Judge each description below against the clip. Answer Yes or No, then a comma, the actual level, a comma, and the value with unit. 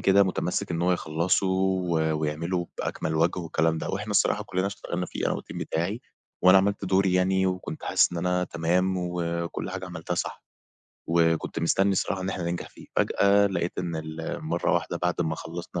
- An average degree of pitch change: No, narrow, 2.1 semitones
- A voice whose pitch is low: Yes, very low, 90 Hz